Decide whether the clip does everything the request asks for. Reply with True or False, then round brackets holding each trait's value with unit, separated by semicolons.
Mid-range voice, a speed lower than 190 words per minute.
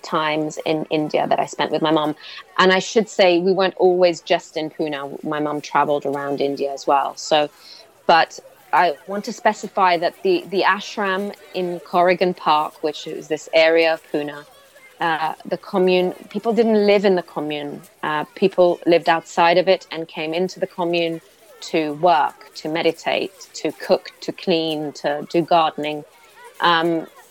True (170 Hz; 170 wpm)